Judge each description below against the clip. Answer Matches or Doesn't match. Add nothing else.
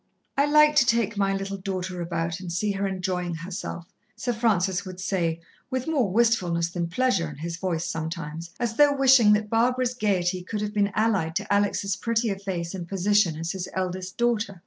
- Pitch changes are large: Doesn't match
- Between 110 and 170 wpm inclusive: Doesn't match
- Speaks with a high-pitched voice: Matches